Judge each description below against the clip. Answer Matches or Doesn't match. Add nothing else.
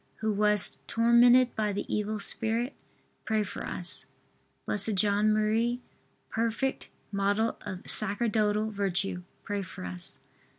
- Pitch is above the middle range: Matches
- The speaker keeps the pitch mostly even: Matches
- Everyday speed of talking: Doesn't match